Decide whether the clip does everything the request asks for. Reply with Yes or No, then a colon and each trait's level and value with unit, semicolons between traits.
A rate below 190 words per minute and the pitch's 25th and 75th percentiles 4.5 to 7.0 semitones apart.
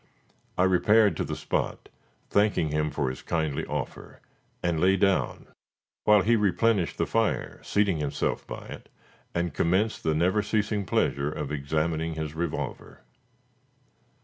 Yes: average, 140 wpm; average, 4.8 semitones